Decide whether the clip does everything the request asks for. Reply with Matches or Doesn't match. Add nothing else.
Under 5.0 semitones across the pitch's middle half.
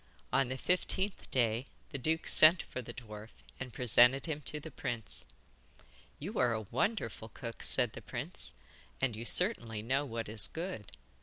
Doesn't match